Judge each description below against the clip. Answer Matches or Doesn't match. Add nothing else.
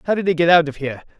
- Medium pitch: Matches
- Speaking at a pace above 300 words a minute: Matches